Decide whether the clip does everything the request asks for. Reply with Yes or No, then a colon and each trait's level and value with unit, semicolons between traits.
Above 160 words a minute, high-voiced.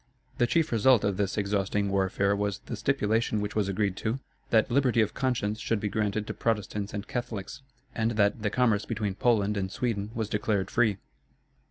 No: average, 185 wpm; low, 105 Hz